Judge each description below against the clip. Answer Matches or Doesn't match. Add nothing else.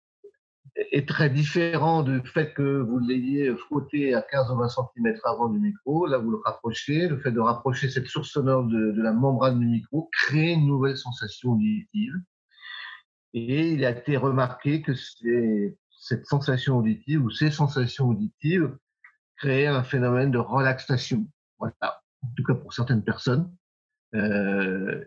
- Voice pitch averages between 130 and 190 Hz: Matches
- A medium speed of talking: Matches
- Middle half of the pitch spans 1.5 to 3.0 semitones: Doesn't match